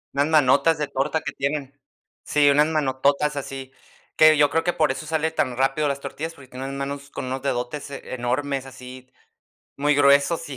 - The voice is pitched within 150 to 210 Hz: No, medium, 140 Hz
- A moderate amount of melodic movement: No, narrow, 2.0 semitones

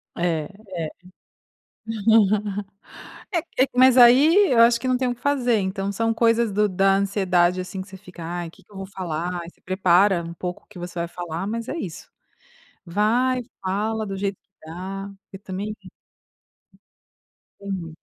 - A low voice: No, high, 195 Hz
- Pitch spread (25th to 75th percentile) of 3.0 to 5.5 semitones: Yes, average, 4.1 semitones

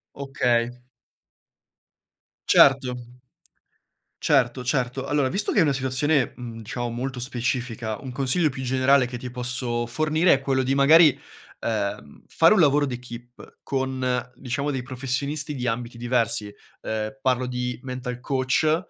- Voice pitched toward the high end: No, low, 130 Hz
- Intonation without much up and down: Yes, narrow, 2.1 semitones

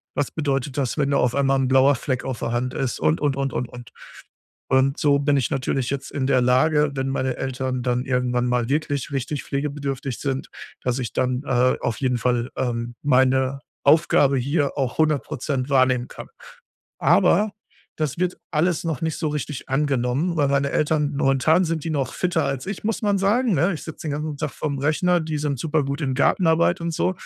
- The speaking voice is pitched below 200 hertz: Yes, medium, 140 Hz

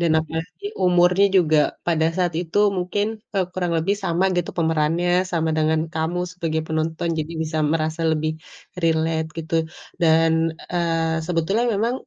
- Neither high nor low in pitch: Yes, medium, 165 Hz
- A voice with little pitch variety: Yes, narrow, 1.9 semitones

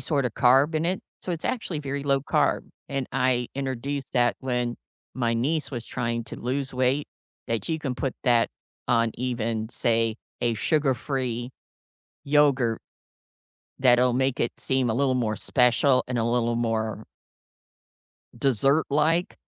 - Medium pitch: No, low, 125 Hz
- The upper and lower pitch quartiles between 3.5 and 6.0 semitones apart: No, average, 2.9 semitones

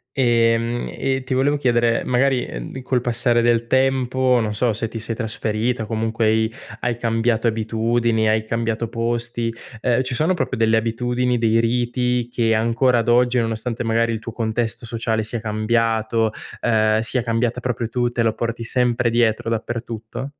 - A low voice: Yes, low, 115 Hz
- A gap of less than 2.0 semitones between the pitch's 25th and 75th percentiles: Yes, narrow, 1.5 semitones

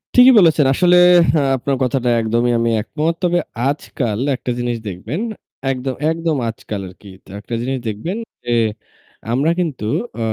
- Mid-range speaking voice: No, low, 130 Hz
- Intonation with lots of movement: Yes, wide, 5.9 semitones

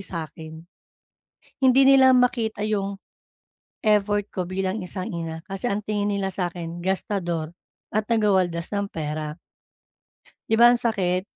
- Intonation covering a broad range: No, average, 3.5 semitones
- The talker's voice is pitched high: Yes, high, 195 Hz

